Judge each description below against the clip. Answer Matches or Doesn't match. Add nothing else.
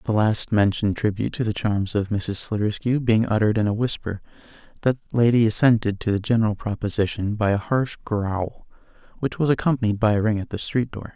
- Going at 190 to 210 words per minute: Matches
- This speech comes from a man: Matches